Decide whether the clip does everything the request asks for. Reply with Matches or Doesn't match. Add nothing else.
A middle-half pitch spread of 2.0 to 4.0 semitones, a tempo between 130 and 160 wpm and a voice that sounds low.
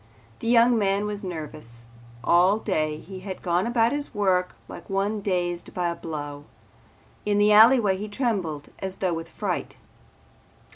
Doesn't match